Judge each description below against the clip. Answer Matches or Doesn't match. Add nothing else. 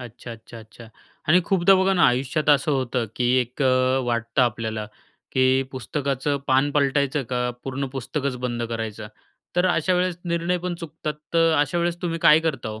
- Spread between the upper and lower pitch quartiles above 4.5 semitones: Matches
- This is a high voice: Doesn't match